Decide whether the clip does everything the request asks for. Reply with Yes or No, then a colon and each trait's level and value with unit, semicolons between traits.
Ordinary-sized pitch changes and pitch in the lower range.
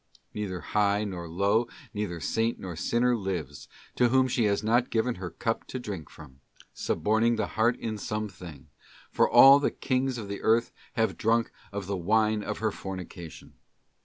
Yes: average, 3.9 semitones; low, 105 Hz